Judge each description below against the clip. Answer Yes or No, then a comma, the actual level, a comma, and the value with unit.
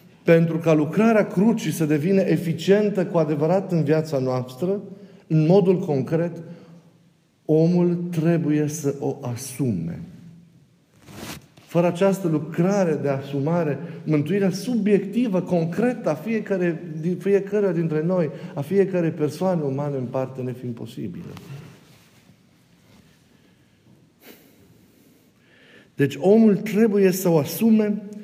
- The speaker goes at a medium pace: No, slow, 105 wpm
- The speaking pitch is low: No, medium, 170 Hz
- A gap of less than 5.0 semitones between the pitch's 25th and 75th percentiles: Yes, average, 4.0 semitones